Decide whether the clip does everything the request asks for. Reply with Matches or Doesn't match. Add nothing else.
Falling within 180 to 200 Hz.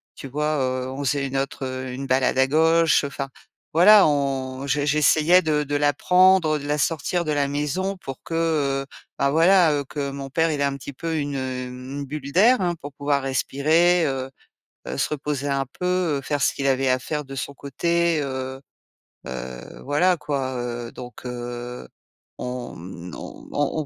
Doesn't match